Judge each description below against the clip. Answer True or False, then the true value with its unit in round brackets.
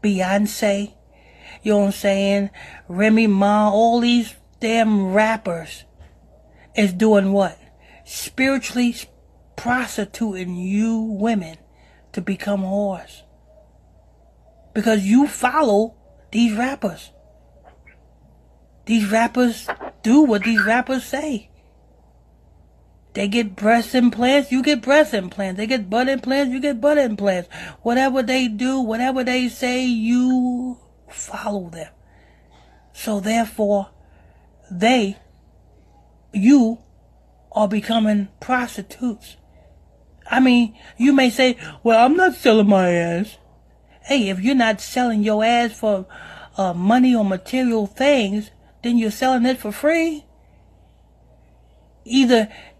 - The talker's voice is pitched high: True (220 Hz)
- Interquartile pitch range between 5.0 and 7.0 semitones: False (4.2 semitones)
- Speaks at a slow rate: True (110 wpm)